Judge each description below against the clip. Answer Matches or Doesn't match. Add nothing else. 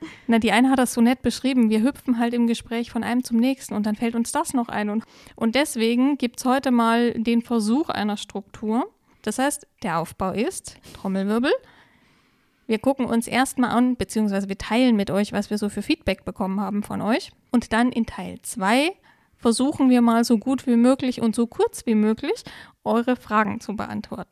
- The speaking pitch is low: Doesn't match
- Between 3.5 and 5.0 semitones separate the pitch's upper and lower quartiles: Doesn't match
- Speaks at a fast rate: Matches